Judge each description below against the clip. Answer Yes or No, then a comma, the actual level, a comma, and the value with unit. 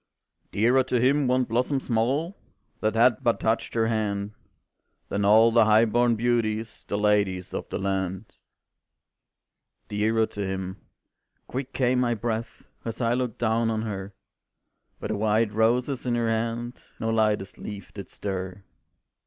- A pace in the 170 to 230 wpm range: No, average, 150 wpm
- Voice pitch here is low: Yes, low, 110 Hz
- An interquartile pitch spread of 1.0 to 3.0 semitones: Yes, narrow, 2.5 semitones